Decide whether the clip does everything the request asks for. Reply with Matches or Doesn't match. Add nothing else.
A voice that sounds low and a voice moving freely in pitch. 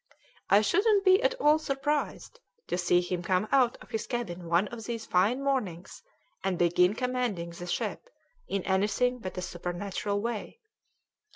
Doesn't match